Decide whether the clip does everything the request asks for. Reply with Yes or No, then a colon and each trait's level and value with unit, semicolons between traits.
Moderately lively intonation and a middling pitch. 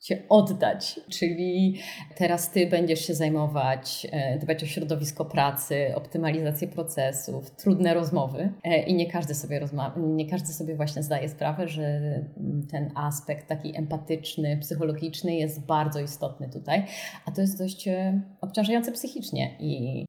Yes: average, 3.1 semitones; medium, 160 Hz